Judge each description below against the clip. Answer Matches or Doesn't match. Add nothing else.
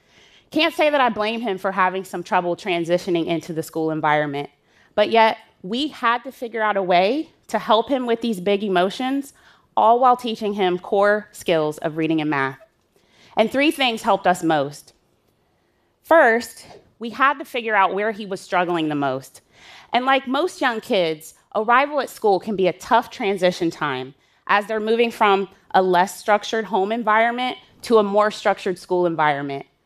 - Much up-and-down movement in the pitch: Doesn't match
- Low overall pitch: Doesn't match